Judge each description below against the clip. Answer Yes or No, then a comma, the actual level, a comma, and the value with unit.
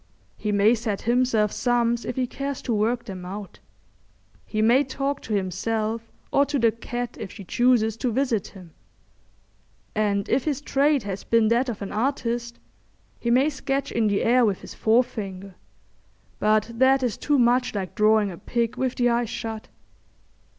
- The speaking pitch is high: Yes, high, 230 Hz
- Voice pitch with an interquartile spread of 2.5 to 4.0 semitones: Yes, average, 2.9 semitones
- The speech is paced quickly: No, average, 170 wpm